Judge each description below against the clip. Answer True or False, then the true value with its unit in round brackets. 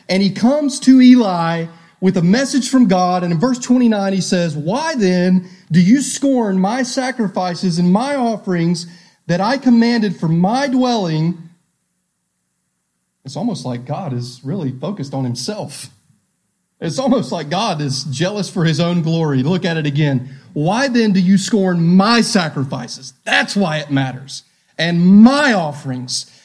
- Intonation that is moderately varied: False (6.4 semitones)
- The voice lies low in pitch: False (180 Hz)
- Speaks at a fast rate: False (155 wpm)